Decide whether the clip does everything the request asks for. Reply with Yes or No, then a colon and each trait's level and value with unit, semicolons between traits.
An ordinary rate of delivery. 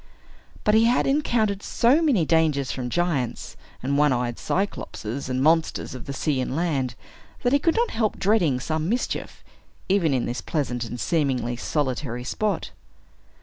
Yes: average, 160 wpm